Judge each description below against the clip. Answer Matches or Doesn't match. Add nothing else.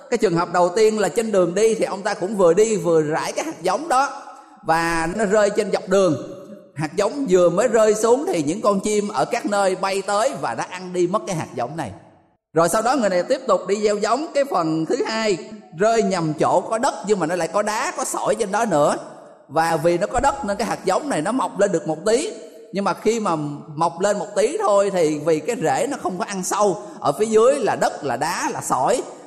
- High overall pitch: Matches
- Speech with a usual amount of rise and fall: Matches